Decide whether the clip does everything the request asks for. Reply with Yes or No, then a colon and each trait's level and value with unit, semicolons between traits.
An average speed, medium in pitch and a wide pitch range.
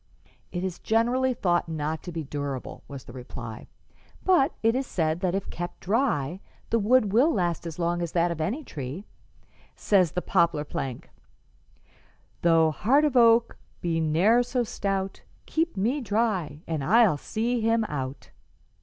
Yes: average, 160 wpm; medium, 180 Hz; wide, 6.5 semitones